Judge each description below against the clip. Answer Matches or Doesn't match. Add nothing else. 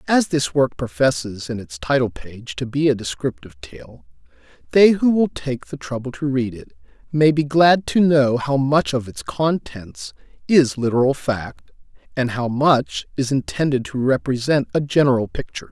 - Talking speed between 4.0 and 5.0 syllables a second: Matches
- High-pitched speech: Doesn't match